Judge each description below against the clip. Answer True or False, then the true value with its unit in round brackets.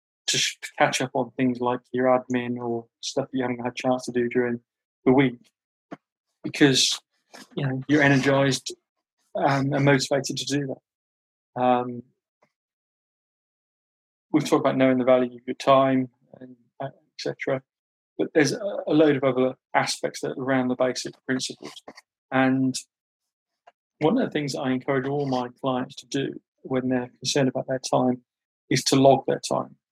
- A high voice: False (130 Hz)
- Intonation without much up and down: True (1.5 semitones)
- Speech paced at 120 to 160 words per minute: True (155 wpm)